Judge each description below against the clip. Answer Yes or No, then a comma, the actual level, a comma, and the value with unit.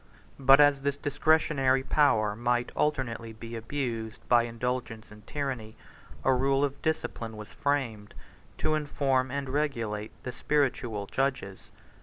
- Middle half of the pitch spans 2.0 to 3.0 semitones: No, average, 3.9 semitones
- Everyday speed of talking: No, slow, 130 wpm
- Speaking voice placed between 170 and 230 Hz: No, low, 130 Hz